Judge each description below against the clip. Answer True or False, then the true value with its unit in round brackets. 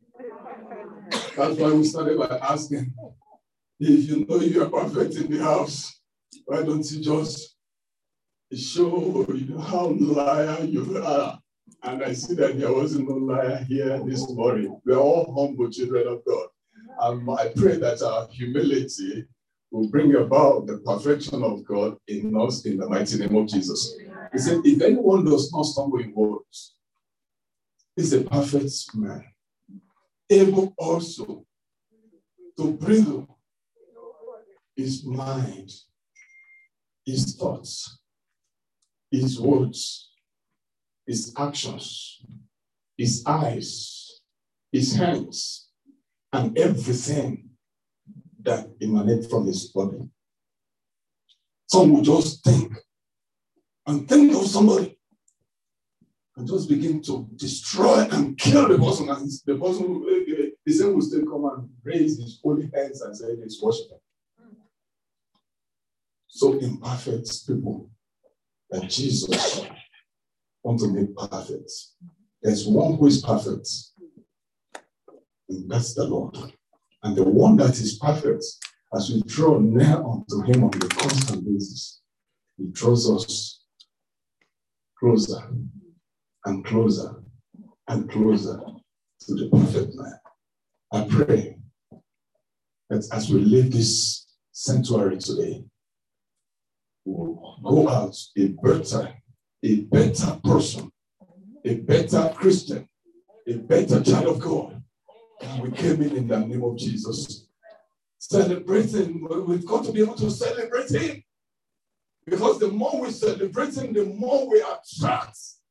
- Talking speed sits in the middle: False (120 wpm)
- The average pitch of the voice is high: False (140 Hz)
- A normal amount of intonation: False (8.6 semitones)